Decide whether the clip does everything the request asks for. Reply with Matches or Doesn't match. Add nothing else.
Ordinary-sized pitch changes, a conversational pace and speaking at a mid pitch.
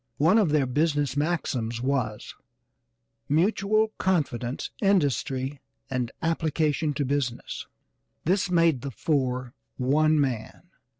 Doesn't match